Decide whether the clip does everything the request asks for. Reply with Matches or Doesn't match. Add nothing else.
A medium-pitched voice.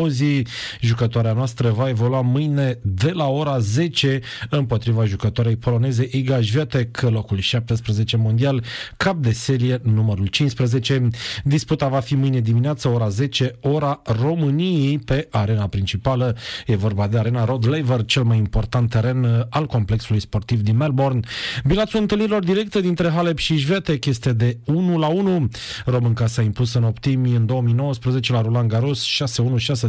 Doesn't match